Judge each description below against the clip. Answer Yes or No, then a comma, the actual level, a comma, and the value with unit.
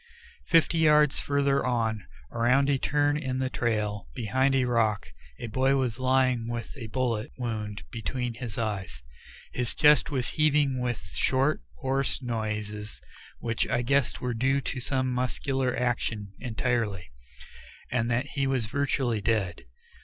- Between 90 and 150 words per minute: Yes, average, 145 wpm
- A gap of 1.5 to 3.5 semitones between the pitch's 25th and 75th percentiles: Yes, average, 3.1 semitones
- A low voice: Yes, low, 125 Hz